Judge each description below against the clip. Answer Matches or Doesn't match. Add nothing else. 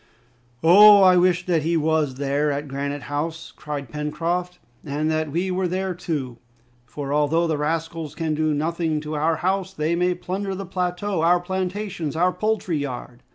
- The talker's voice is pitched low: Doesn't match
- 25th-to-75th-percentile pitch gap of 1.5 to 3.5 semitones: Matches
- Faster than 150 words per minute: Matches